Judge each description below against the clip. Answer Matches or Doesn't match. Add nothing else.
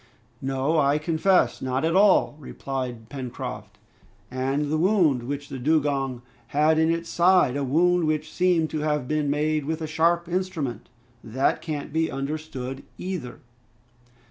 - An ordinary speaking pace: Matches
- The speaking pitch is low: Doesn't match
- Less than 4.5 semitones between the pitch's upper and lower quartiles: Matches